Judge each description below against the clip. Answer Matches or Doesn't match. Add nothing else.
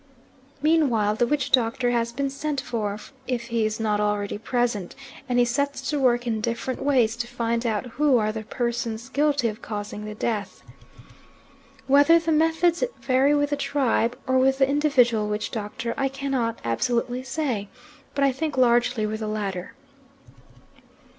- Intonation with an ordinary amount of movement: Matches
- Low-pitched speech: Doesn't match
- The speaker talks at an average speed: Matches